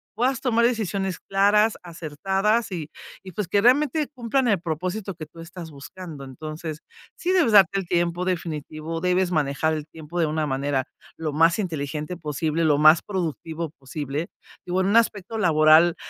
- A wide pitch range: No, average, 4.3 semitones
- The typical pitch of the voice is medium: Yes, medium, 170 Hz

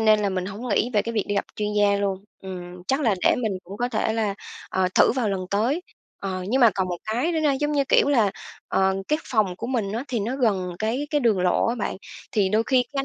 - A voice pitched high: Yes, high, 215 Hz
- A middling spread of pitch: Yes, average, 4.1 semitones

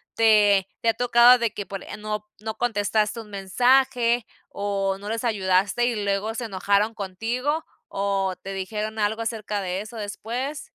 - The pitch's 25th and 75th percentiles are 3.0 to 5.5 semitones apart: No, narrow, 2.6 semitones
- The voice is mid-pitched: No, high, 215 Hz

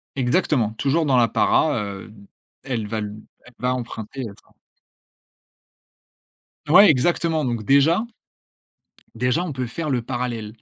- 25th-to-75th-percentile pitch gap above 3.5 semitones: Yes, average, 4.9 semitones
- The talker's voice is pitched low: Yes, low, 125 Hz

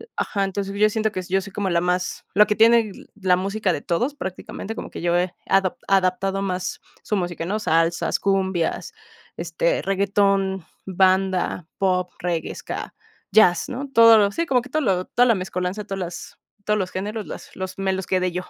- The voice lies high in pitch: Yes, high, 195 Hz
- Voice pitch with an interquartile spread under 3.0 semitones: Yes, narrow, 2.5 semitones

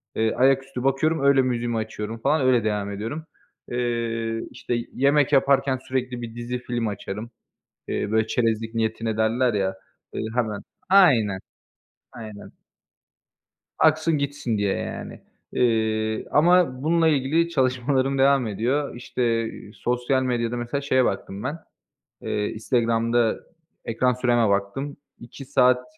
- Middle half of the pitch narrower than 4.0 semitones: Yes, average, 3.3 semitones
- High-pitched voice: No, low, 120 Hz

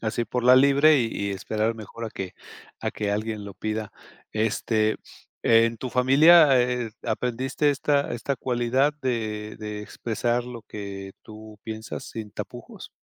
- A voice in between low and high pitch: No, low, 115 Hz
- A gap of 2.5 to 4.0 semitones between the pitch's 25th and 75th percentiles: Yes, average, 2.8 semitones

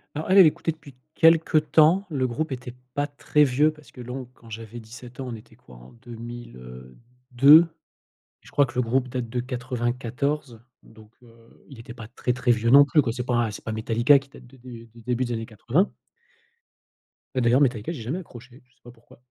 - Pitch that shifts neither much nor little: Yes, average, 3.3 semitones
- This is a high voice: No, low, 125 Hz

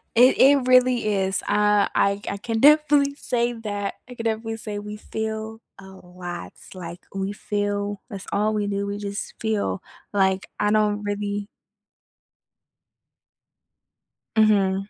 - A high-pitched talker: Yes, high, 205 Hz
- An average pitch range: No, narrow, 1.9 semitones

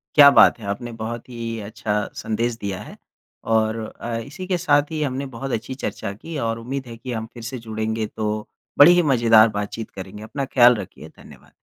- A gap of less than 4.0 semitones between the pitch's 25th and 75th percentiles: Yes, average, 3.4 semitones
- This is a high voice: No, low, 115 Hz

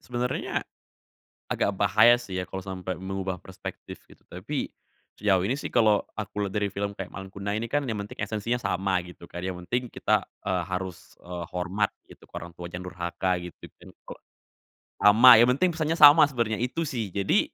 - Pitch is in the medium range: No, low, 100 Hz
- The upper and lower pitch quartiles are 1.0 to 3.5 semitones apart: No, average, 4.2 semitones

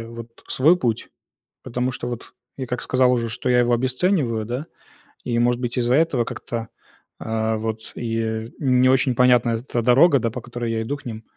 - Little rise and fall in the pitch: Yes, narrow, 1.9 semitones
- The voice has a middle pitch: No, low, 120 Hz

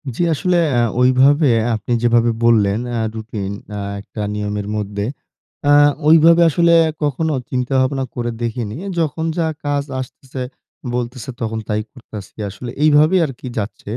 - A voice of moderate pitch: No, low, 125 Hz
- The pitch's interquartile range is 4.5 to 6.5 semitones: Yes, average, 5.0 semitones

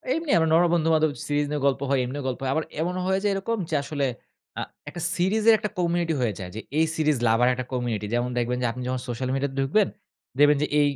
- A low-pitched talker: No, medium, 145 Hz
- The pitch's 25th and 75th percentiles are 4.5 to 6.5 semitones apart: Yes, average, 5.3 semitones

